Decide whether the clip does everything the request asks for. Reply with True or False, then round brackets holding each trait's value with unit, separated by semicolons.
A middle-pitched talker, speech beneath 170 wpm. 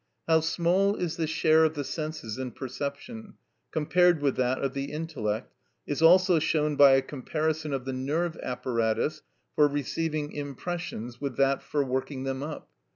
True (150 Hz; 160 wpm)